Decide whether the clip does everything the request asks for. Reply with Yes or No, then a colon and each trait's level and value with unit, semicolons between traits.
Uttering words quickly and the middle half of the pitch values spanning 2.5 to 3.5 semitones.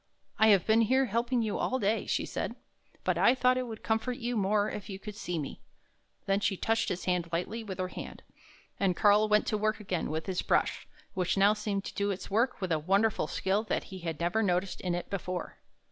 Yes: fast, 240 wpm; average, 3.2 semitones